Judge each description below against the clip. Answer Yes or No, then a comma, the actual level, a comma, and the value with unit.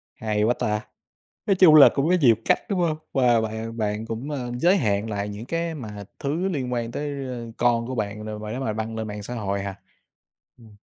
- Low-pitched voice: Yes, low, 115 Hz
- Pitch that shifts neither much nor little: Yes, average, 4.5 semitones